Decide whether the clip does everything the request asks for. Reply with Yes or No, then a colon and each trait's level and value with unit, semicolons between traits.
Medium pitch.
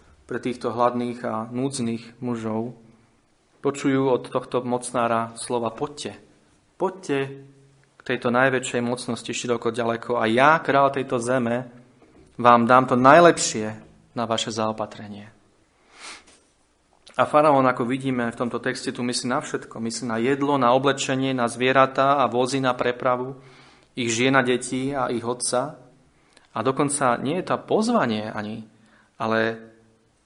No: low, 125 Hz